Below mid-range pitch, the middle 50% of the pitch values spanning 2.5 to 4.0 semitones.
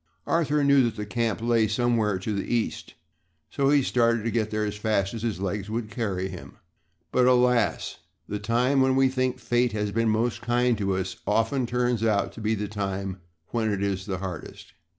Yes: low, 110 Hz; average, 3.1 semitones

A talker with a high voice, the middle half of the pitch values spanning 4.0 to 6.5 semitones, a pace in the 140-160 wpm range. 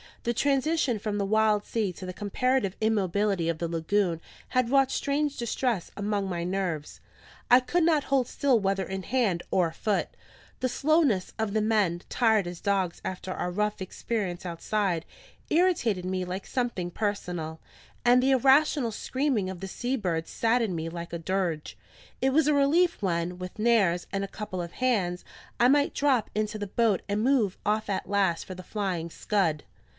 No: high, 205 Hz; average, 5.2 semitones; average, 175 wpm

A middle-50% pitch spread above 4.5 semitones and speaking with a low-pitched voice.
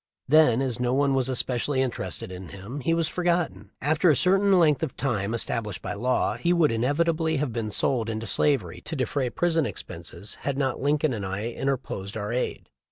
Yes: wide, 5.4 semitones; low, 130 Hz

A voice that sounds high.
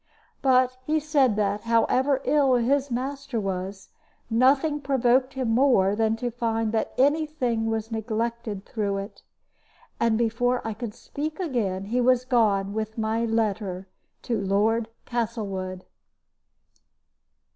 Yes: high, 230 Hz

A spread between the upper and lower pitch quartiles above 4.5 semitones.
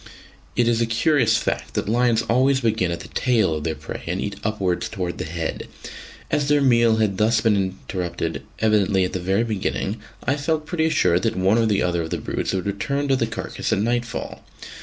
No: average, 4.2 semitones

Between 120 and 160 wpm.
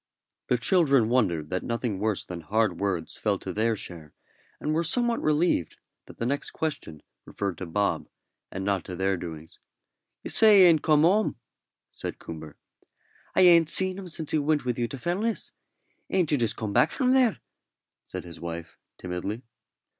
No: average, 175 wpm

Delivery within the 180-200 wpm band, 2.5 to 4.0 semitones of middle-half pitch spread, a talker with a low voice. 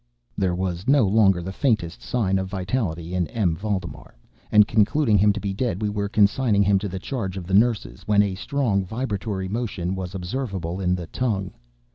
Yes: average, 190 wpm; average, 2.9 semitones; low, 100 Hz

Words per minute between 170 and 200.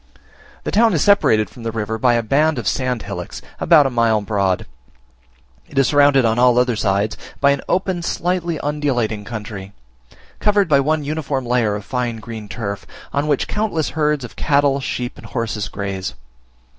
Yes: average, 175 wpm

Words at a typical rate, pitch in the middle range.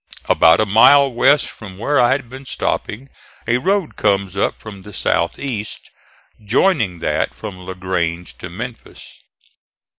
No: average, 145 wpm; low, 110 Hz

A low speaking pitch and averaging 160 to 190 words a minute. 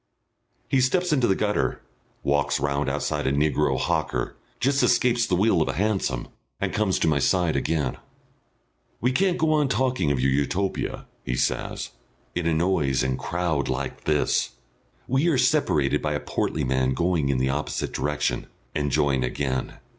Yes: very low, 80 Hz; average, 170 wpm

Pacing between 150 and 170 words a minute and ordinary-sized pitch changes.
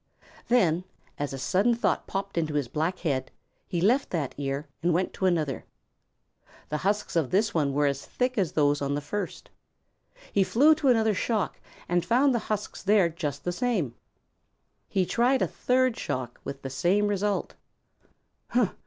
No: average, 165 wpm; wide, 6.7 semitones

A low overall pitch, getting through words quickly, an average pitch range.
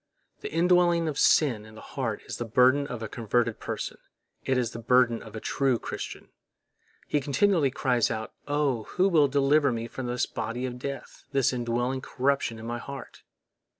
No: low, 125 Hz; average, 185 wpm; average, 3.2 semitones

